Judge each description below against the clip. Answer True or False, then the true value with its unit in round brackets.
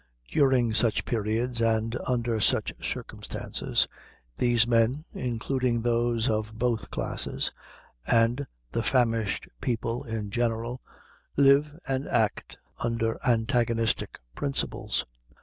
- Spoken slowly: True (100 wpm)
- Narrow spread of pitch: True (1.7 semitones)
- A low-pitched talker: True (115 Hz)